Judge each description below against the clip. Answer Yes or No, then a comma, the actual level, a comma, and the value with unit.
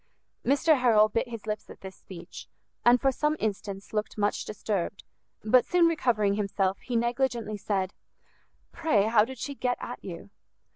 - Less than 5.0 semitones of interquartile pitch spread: Yes, average, 3.8 semitones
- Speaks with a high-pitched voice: Yes, high, 220 Hz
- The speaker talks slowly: No, average, 160 wpm